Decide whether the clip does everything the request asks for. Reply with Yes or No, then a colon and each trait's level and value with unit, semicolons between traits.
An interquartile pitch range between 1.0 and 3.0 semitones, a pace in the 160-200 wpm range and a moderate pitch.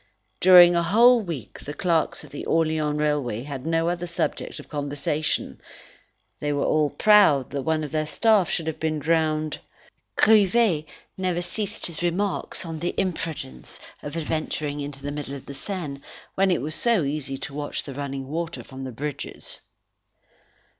No: average, 3.4 semitones; average, 165 wpm; medium, 155 Hz